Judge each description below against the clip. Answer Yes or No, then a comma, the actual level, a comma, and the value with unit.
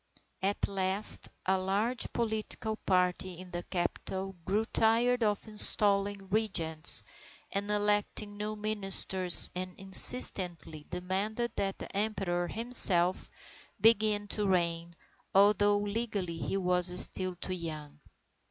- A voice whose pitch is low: No, high, 195 Hz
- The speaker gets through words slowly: Yes, slow, 115 wpm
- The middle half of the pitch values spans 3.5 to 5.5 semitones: No, average, 2.7 semitones